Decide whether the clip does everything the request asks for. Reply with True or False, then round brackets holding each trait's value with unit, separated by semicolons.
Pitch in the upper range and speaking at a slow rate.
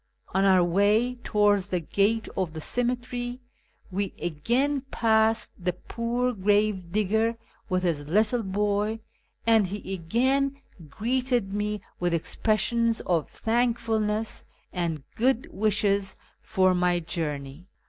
True (210 Hz; 115 wpm)